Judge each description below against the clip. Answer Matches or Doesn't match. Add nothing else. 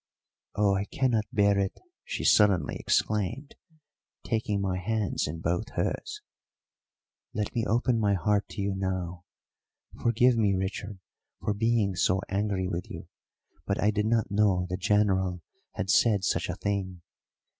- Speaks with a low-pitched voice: Matches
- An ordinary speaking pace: Matches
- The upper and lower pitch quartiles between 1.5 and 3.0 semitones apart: Matches